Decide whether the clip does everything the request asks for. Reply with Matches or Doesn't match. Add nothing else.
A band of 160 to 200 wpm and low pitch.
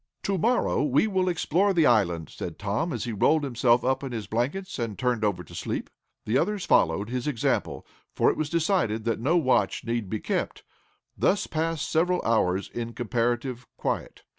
Matches